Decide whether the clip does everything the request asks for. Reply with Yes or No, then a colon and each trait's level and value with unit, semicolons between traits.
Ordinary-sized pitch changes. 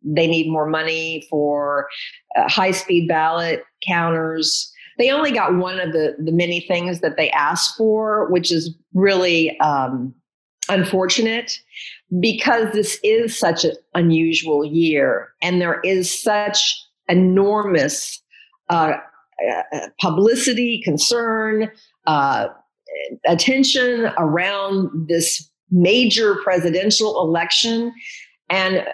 Yes: average, 5.0 semitones